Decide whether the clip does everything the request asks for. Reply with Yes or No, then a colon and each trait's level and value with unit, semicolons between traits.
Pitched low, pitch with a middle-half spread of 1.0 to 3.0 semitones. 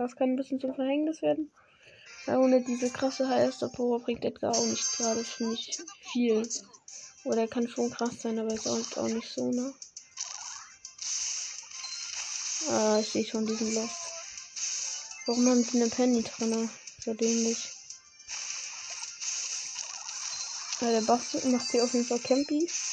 No: high, 240 Hz; narrow, 2.5 semitones